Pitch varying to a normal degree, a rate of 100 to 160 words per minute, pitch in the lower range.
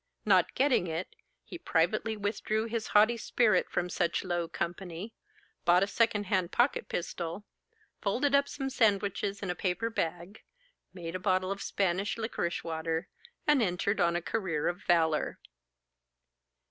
No: average, 4.0 semitones; average, 145 wpm; high, 190 Hz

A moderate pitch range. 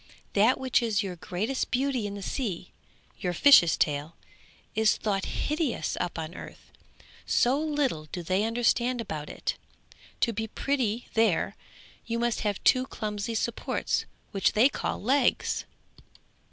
Yes: average, 4.7 semitones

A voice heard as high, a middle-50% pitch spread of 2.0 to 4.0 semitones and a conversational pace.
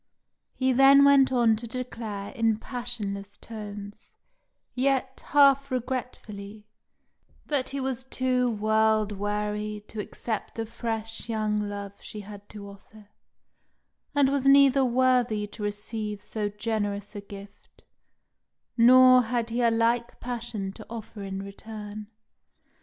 No: high, 225 Hz; average, 3.4 semitones; slow, 125 wpm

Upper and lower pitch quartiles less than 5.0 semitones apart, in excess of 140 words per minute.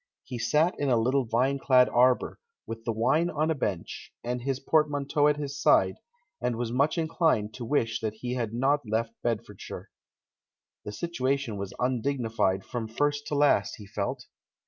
Yes: average, 4.1 semitones; average, 170 wpm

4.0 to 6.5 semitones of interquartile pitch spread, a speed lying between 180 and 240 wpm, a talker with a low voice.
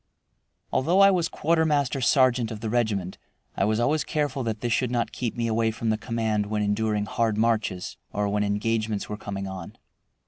No: average, 3.2 semitones; average, 185 wpm; low, 115 Hz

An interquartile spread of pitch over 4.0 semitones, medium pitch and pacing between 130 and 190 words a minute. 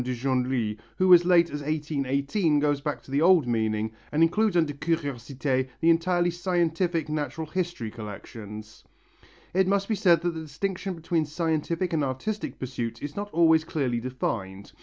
Yes: average, 5.0 semitones; medium, 155 Hz; average, 160 wpm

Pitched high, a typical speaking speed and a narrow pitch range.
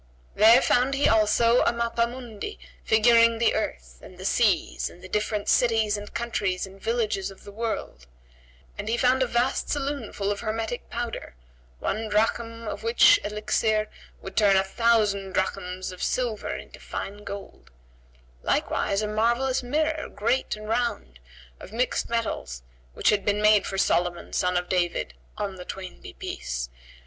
No: high, 215 Hz; average, 160 wpm; average, 3.3 semitones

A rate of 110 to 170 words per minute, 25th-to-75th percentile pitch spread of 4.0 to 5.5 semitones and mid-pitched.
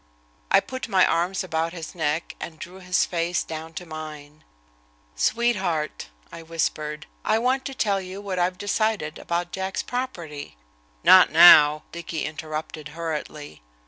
No: average, 145 wpm; average, 3.4 semitones; medium, 170 Hz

